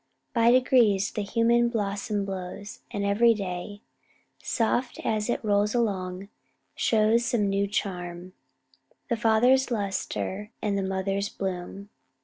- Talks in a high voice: Yes, high, 205 Hz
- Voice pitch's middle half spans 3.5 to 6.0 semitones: No, average, 2.8 semitones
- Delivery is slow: Yes, slow, 125 wpm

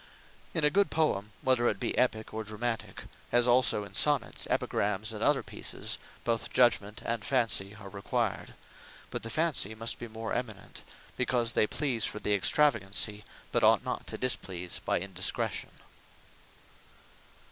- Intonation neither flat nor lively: Yes, average, 3.1 semitones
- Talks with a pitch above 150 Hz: No, low, 115 Hz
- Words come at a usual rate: Yes, average, 150 wpm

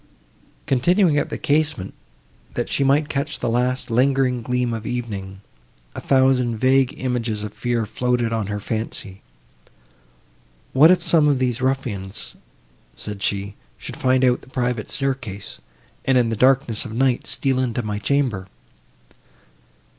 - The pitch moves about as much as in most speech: Yes, average, 3.3 semitones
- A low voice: Yes, low, 125 Hz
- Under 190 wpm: Yes, average, 145 wpm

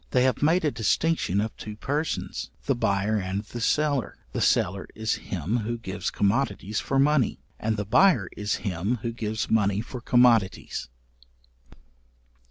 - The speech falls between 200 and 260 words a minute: No, average, 155 wpm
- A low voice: Yes, low, 110 Hz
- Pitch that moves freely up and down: No, average, 4.0 semitones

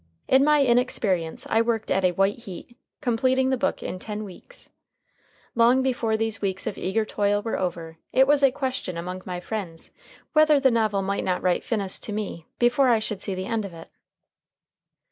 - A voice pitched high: Yes, high, 215 Hz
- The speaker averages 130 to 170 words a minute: No, average, 190 wpm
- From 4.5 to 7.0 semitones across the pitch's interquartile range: Yes, average, 4.9 semitones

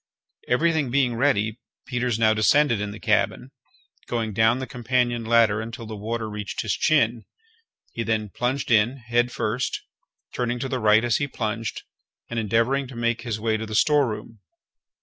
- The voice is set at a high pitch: No, low, 115 Hz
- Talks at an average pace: Yes, average, 170 wpm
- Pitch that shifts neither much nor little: No, narrow, 2.3 semitones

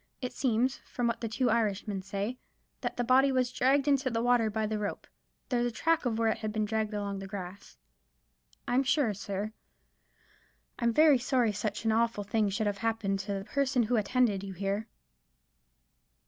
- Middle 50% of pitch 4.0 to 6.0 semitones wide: No, average, 3.5 semitones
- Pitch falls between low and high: No, high, 225 Hz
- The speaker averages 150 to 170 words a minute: No, average, 190 wpm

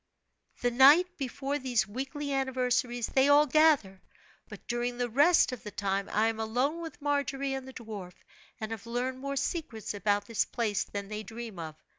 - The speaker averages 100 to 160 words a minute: No, average, 180 wpm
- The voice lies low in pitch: No, high, 245 Hz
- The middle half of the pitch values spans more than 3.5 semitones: Yes, average, 4.1 semitones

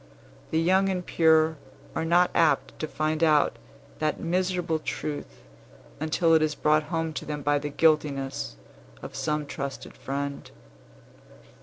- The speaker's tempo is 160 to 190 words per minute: No, average, 140 wpm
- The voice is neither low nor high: Yes, medium, 155 Hz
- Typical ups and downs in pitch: No, narrow, 1.9 semitones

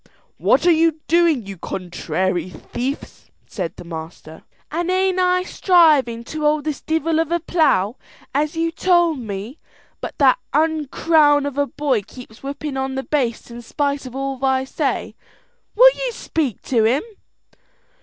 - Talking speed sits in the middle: Yes, average, 155 wpm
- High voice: Yes, very high, 285 Hz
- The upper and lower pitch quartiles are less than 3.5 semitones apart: No, average, 5.2 semitones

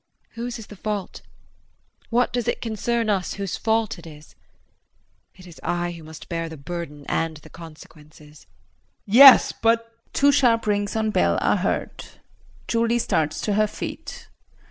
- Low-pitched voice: No, high, 200 Hz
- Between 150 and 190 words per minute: Yes, average, 160 wpm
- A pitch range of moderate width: No, wide, 5.7 semitones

